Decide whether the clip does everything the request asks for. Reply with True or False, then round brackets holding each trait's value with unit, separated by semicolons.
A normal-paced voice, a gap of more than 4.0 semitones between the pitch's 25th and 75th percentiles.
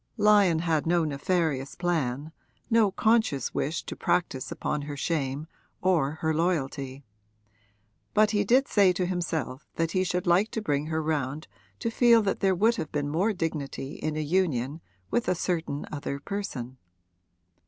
True (160 wpm; 4.6 semitones)